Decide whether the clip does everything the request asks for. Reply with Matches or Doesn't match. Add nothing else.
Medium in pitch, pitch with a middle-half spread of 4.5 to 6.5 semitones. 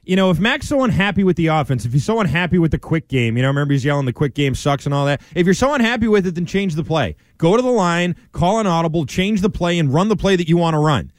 Matches